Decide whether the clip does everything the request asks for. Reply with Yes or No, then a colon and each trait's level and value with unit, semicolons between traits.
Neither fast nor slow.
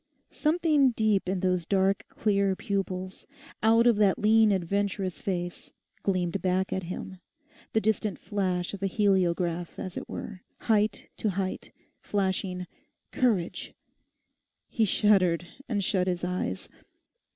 No: slow, 130 wpm